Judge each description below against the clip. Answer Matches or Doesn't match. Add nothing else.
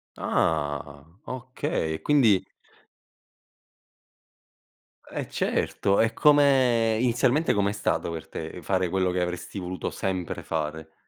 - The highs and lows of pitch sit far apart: Matches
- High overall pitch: Doesn't match